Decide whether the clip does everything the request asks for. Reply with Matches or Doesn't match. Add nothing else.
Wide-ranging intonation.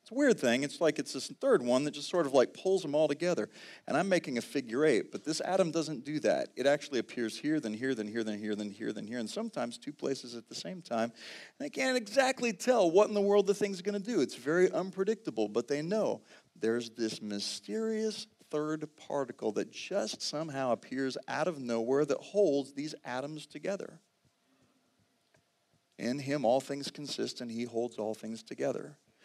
Matches